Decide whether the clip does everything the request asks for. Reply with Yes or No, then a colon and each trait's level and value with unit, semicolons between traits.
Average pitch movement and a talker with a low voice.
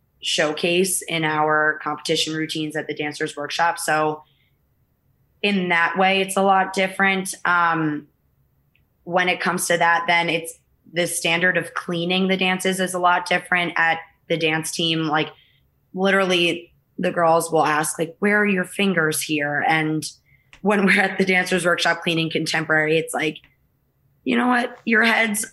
No: average, 3.0 semitones; medium, 170 Hz